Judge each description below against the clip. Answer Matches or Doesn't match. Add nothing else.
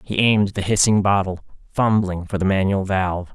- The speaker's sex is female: Doesn't match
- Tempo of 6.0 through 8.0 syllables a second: Doesn't match